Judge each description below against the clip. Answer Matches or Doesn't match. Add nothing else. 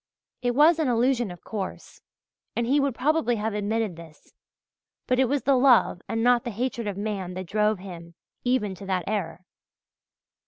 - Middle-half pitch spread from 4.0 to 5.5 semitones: Matches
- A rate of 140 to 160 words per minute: Doesn't match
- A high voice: Matches